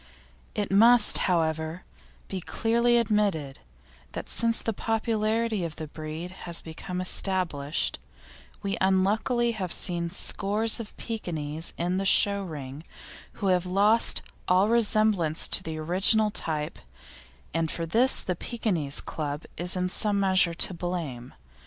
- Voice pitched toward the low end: No, medium, 185 Hz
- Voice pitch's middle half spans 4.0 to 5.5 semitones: Yes, average, 4.7 semitones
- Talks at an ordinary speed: No, slow, 130 wpm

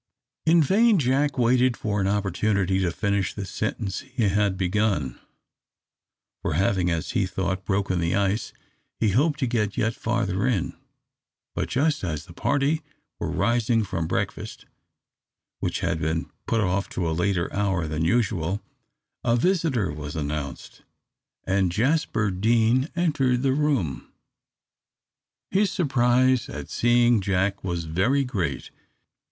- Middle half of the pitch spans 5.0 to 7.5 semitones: Yes, wide, 5.5 semitones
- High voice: No, low, 105 Hz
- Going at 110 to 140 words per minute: Yes, slow, 135 wpm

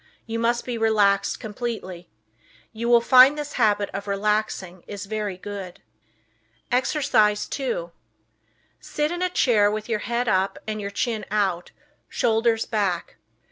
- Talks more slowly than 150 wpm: Yes, average, 140 wpm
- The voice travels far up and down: No, average, 3.0 semitones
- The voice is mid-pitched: No, high, 215 Hz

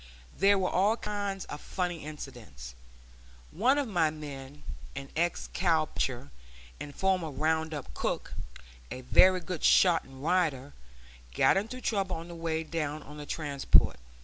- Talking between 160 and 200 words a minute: No, average, 150 wpm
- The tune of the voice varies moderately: Yes, average, 4.3 semitones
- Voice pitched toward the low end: No, medium, 160 Hz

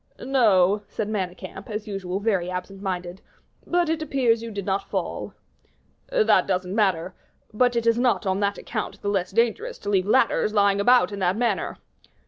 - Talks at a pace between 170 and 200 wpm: Yes, average, 175 wpm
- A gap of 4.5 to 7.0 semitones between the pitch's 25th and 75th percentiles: No, average, 3.4 semitones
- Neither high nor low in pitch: No, high, 205 Hz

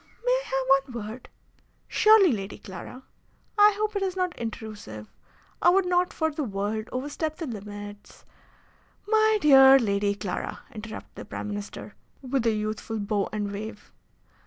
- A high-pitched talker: Yes, high, 235 Hz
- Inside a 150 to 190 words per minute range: Yes, average, 160 wpm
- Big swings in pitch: Yes, wide, 8.6 semitones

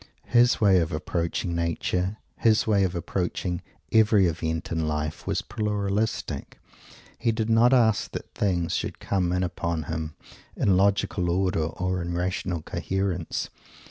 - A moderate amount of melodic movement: Yes, average, 3.3 semitones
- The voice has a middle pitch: No, very low, 90 Hz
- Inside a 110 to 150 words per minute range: Yes, average, 140 wpm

